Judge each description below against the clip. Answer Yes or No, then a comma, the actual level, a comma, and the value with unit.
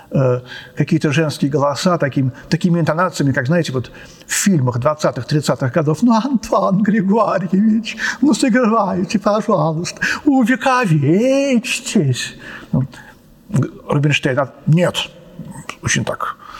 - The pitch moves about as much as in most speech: No, wide, 6.5 semitones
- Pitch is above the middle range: No, medium, 175 Hz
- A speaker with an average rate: No, slow, 90 wpm